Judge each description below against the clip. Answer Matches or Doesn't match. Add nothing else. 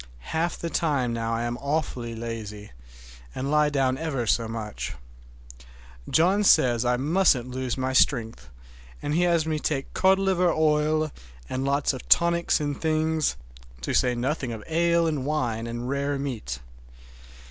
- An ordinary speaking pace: Matches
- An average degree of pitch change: Matches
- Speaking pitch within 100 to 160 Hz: Matches